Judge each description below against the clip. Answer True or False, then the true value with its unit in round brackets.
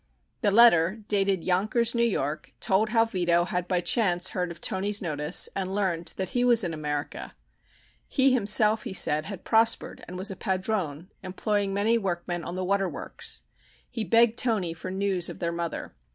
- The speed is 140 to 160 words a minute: False (180 wpm)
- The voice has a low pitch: False (190 Hz)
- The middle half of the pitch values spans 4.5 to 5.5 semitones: False (3.8 semitones)